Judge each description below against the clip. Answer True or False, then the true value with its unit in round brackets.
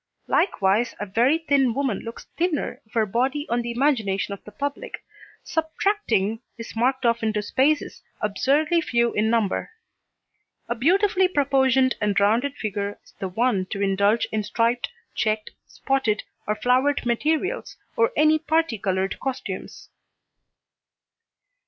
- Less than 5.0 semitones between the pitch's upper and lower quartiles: False (5.3 semitones)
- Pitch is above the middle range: True (240 Hz)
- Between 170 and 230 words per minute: False (135 wpm)